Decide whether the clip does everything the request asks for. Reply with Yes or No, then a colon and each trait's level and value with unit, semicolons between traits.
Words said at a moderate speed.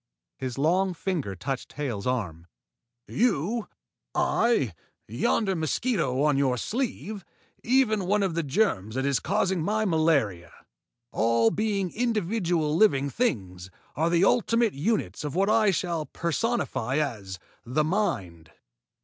No: slow, 125 wpm